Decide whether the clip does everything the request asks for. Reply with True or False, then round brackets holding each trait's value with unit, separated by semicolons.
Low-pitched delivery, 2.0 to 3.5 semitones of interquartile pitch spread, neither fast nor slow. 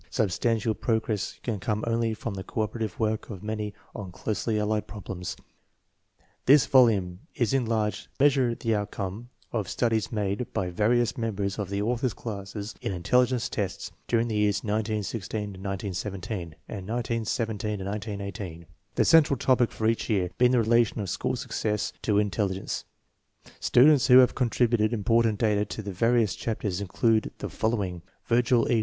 True (110 Hz; 2.6 semitones; 155 wpm)